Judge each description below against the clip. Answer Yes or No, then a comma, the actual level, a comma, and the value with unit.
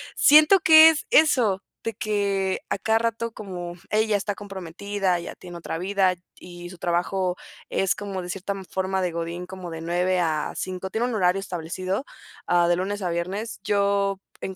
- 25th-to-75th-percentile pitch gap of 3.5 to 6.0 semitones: No, narrow, 2.5 semitones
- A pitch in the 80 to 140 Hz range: No, high, 190 Hz